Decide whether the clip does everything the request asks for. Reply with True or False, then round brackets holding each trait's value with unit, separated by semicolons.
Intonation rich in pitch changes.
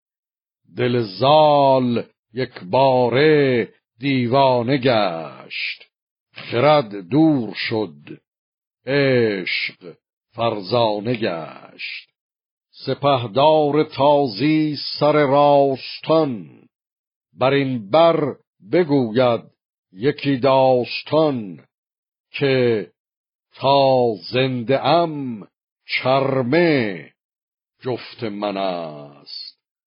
False (3.5 semitones)